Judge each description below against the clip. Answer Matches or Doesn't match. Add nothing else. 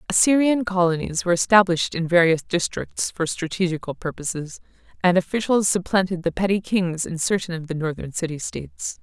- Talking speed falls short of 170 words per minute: Matches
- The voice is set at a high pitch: Doesn't match